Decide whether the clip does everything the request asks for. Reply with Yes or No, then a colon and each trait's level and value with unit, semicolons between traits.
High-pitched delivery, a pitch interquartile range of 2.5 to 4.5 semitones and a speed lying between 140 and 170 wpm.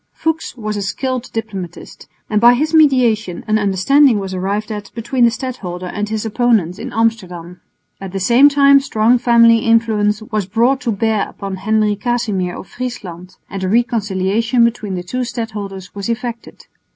Yes: high, 220 Hz; average, 3.5 semitones; average, 165 wpm